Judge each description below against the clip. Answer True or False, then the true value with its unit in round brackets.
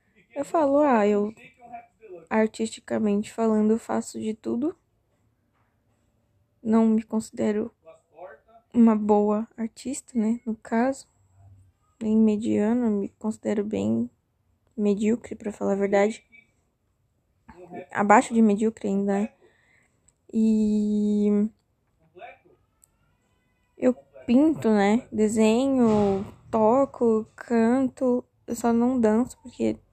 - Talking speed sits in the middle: False (90 wpm)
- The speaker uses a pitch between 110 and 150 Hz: False (215 Hz)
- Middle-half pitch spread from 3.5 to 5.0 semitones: False (2.8 semitones)